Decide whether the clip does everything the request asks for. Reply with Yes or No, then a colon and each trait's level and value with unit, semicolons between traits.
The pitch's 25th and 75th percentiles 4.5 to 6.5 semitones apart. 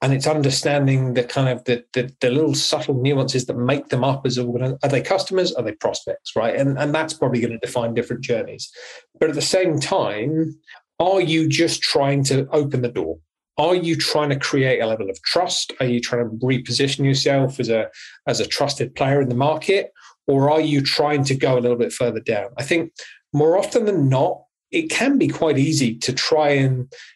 No: average, 3.4 semitones